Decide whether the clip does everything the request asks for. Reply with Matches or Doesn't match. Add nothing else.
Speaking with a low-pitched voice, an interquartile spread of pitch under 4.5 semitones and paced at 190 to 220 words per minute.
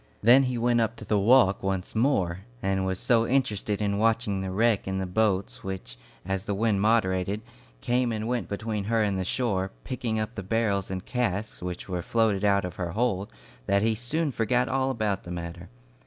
Matches